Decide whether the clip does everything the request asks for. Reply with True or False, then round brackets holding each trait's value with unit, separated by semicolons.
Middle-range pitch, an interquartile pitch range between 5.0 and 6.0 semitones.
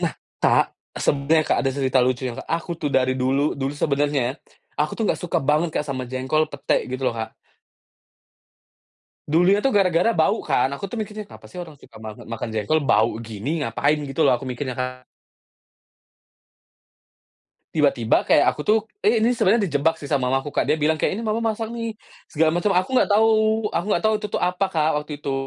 True (150 Hz; 5.6 semitones)